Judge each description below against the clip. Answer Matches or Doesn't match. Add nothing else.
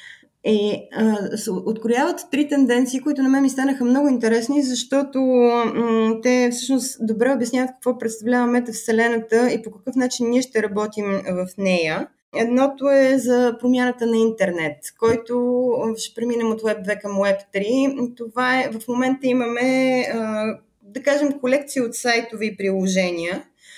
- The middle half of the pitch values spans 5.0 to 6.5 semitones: Doesn't match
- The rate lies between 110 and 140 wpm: Doesn't match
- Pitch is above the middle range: Matches